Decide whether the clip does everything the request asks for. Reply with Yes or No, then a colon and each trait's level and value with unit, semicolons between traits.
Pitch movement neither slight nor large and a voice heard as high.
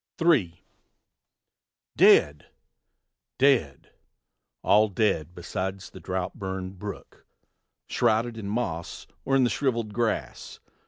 No: average, 4.4 semitones; low, 100 Hz